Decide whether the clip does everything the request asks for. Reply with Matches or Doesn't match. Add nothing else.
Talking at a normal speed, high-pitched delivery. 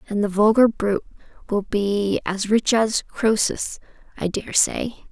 Matches